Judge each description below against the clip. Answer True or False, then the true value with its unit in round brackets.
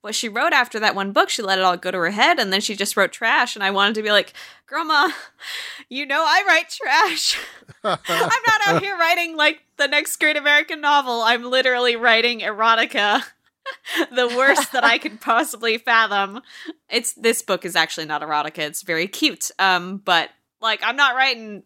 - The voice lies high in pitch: True (235 Hz)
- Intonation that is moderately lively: False (6.6 semitones)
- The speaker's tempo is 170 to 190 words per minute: False (200 wpm)